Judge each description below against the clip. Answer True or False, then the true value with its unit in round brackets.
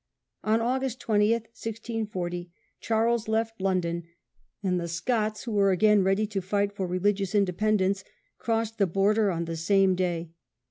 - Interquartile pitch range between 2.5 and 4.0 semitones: True (3.2 semitones)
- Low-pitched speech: False (205 Hz)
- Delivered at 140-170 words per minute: True (155 wpm)